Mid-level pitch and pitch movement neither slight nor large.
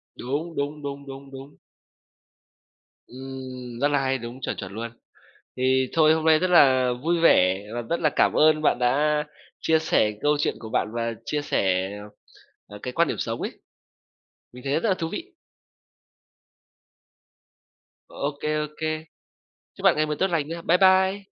Yes: medium, 145 Hz; average, 4.0 semitones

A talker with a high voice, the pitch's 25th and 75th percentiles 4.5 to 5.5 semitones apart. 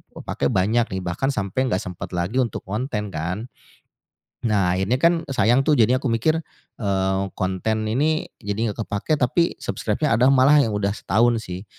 No: low, 110 Hz; average, 5.0 semitones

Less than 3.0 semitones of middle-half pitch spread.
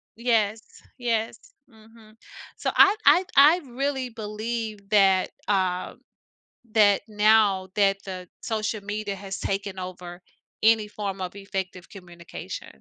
Yes: narrow, 2.6 semitones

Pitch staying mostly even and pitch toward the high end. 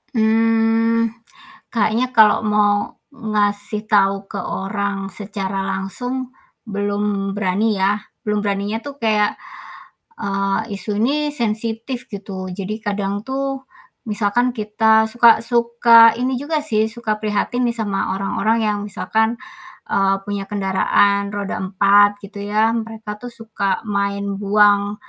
Yes: narrow, 2.1 semitones; high, 210 Hz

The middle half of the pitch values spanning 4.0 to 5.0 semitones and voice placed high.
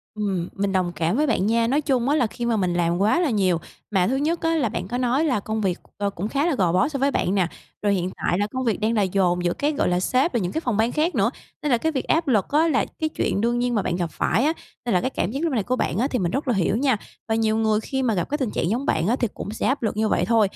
No: wide, 5.5 semitones; high, 225 Hz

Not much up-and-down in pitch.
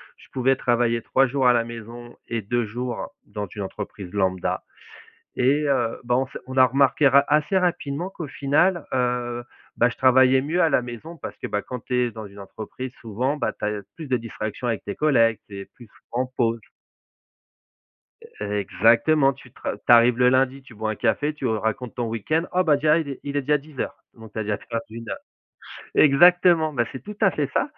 No: average, 3.7 semitones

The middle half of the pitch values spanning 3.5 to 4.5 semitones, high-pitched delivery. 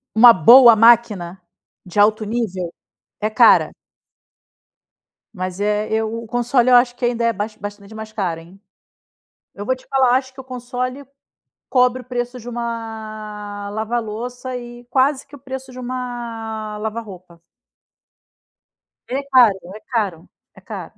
No: average, 3.0 semitones; high, 230 Hz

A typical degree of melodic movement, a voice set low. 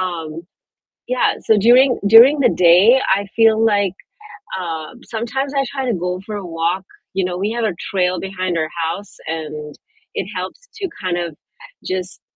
No: average, 4.5 semitones; high, 190 Hz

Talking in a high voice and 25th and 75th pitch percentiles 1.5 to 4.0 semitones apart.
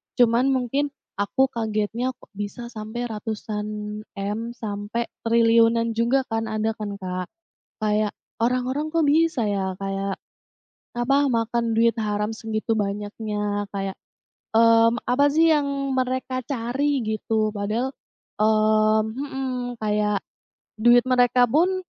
Yes: high, 230 Hz; average, 3.1 semitones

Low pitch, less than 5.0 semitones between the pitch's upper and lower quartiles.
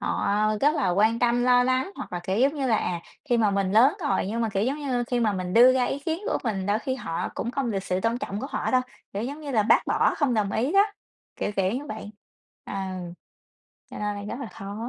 No: high, 235 Hz; average, 4.3 semitones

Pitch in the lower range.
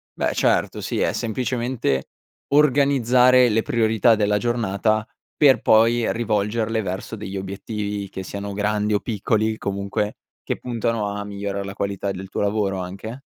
Yes: low, 105 Hz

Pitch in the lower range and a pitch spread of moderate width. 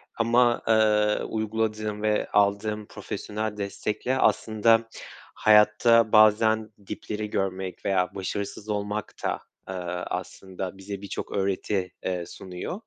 No: low, 105 Hz; narrow, 1.7 semitones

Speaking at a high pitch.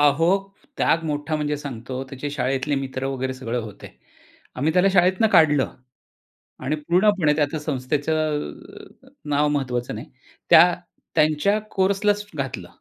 No: medium, 145 Hz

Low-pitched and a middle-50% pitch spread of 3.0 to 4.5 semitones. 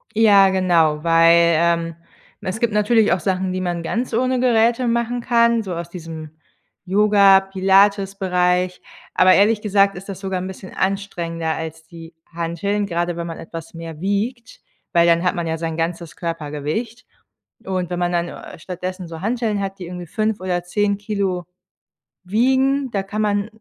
No: medium, 185 Hz; average, 3.5 semitones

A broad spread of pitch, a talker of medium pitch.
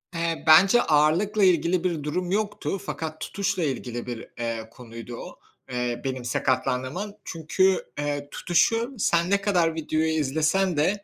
Yes: wide, 6.0 semitones; medium, 160 Hz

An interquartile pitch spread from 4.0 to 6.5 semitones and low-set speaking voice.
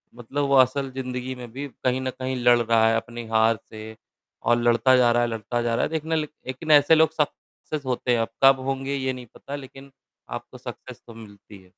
No: average, 2.8 semitones; low, 125 Hz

